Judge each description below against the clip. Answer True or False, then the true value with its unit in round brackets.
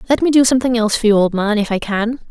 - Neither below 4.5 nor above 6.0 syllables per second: False (7.4 syllables/s)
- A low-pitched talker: False (230 Hz)